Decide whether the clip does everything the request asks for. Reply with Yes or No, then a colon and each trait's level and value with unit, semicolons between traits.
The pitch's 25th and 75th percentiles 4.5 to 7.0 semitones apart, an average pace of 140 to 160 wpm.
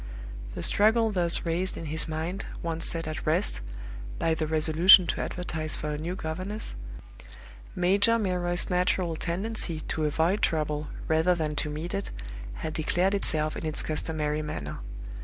No: average, 2.8 semitones; average, 155 wpm